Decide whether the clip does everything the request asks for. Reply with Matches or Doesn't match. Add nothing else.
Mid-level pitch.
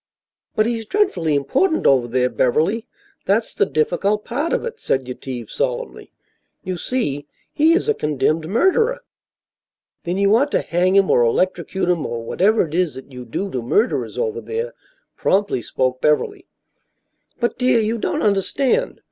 Doesn't match